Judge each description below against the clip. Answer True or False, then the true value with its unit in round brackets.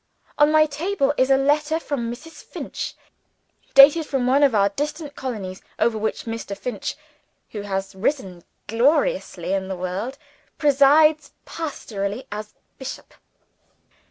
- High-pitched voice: True (265 Hz)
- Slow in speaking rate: True (130 wpm)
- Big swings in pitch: True (6.3 semitones)